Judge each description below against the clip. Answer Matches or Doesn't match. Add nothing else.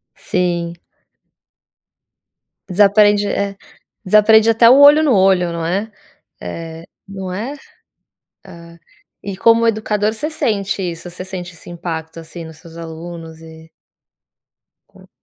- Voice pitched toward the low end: Doesn't match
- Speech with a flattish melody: Doesn't match